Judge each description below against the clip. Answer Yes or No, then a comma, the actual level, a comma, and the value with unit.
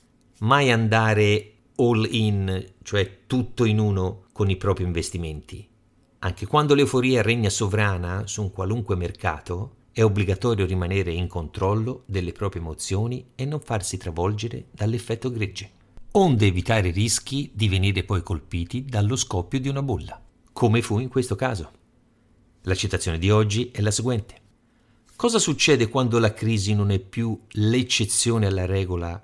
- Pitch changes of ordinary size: Yes, average, 3.7 semitones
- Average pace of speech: Yes, average, 145 wpm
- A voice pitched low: Yes, low, 110 Hz